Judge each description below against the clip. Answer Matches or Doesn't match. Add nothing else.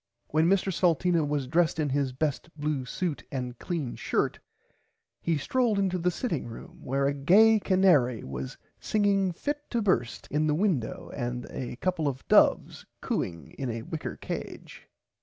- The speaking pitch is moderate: Matches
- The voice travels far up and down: Matches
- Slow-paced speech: Doesn't match